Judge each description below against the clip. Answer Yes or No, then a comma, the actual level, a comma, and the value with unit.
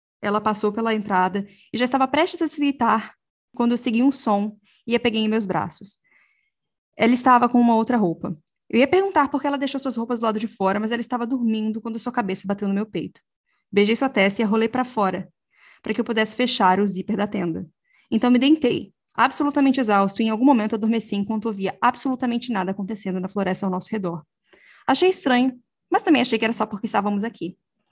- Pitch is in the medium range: No, high, 225 Hz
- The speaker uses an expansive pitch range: No, average, 3.7 semitones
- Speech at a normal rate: No, fast, 215 wpm